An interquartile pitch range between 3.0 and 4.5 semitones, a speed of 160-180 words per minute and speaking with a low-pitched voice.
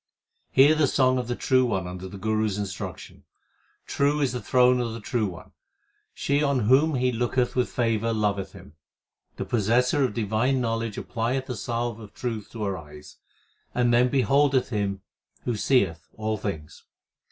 Yes: average, 3.6 semitones; average, 175 wpm; low, 115 Hz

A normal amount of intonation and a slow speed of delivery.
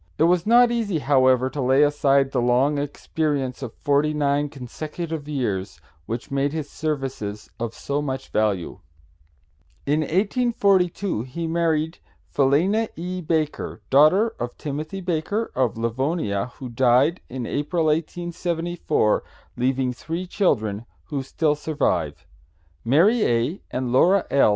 Yes: average, 4.7 semitones; slow, 130 wpm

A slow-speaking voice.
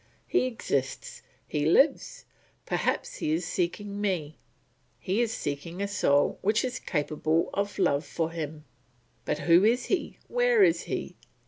No: average, 145 wpm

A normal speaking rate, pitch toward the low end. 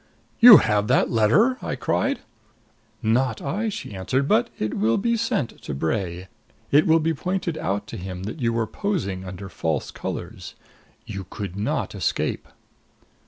Yes: average, 160 wpm; low, 115 Hz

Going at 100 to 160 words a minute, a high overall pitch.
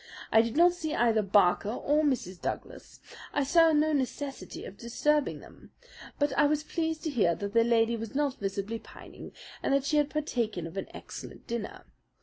No: average, 185 wpm; very high, 255 Hz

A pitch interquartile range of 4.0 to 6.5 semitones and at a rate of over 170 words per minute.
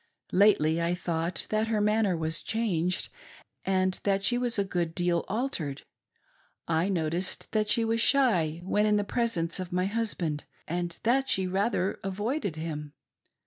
No: average, 4.3 semitones; average, 155 wpm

